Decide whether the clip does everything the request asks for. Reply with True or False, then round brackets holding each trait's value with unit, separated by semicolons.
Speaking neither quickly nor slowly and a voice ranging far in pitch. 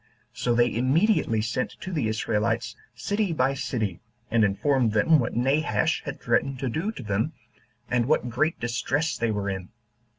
False (165 wpm; 4.8 semitones)